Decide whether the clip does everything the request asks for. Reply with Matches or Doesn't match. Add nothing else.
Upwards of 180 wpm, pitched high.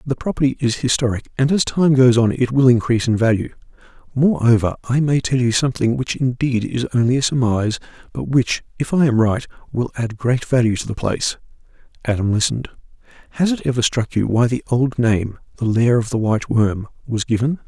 Doesn't match